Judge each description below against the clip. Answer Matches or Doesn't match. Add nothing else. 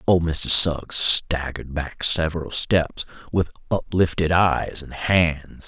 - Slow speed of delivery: Matches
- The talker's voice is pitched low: Matches